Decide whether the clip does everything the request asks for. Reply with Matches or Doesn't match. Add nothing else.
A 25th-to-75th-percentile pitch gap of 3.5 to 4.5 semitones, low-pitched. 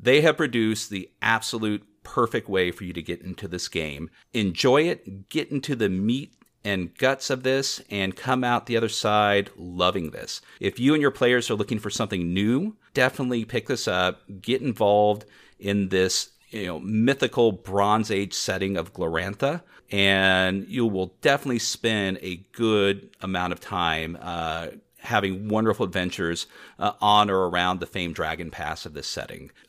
Matches